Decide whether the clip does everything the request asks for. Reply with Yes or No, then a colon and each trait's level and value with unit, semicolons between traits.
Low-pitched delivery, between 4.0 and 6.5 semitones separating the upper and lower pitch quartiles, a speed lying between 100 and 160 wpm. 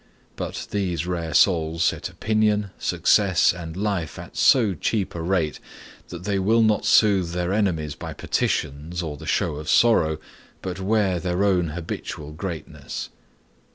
No: very low, 90 Hz; average, 3.6 semitones; average, 150 wpm